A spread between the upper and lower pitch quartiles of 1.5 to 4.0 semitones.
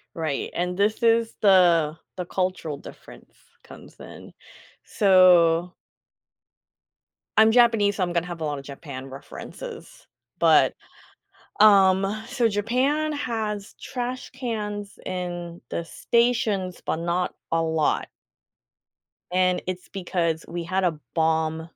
No: average, 4.5 semitones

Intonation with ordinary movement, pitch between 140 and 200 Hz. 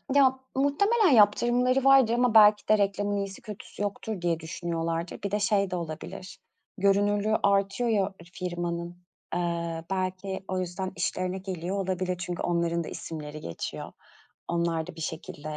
Yes: average, 3.4 semitones; high, 190 Hz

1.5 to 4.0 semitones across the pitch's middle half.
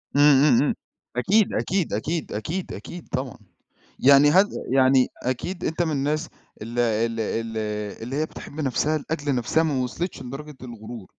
No: average, 4.5 semitones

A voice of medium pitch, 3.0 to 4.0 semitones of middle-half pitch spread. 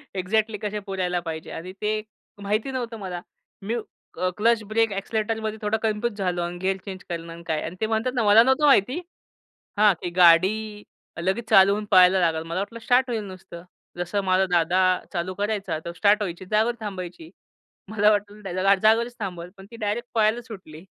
No: high, 205 Hz; average, 3.3 semitones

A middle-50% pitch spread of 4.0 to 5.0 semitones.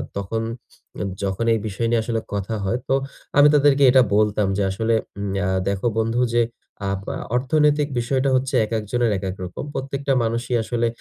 Yes: average, 4.3 semitones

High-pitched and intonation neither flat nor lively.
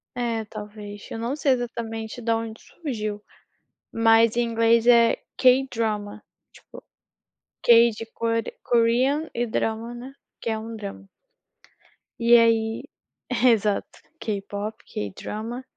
No: high, 230 Hz; narrow, 1.6 semitones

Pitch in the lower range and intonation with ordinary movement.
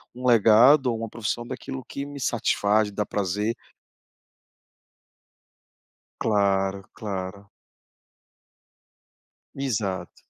Yes: low, 110 Hz; average, 3.5 semitones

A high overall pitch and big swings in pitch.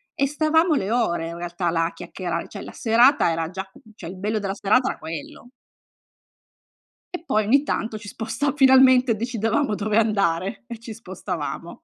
Yes: high, 215 Hz; wide, 5.7 semitones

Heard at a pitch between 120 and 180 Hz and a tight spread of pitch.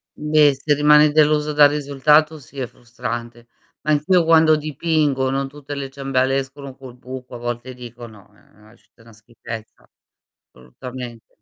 No: low, 135 Hz; average, 3.7 semitones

